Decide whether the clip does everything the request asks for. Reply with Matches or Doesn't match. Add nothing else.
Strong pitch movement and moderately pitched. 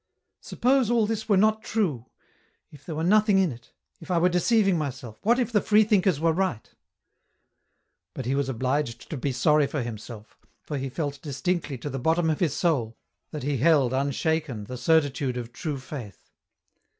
Matches